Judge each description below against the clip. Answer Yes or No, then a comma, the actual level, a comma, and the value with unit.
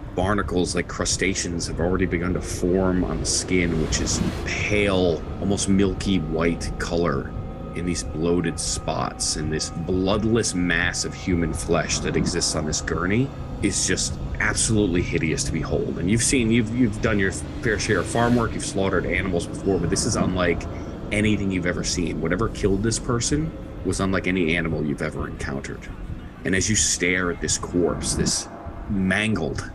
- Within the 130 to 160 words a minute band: No, average, 170 wpm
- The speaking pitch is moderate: No, very low, 90 Hz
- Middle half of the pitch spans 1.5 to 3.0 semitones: No, average, 3.6 semitones